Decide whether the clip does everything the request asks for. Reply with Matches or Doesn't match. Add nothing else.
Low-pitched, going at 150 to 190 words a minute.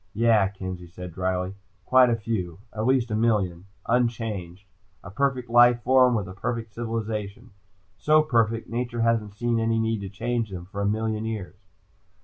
Matches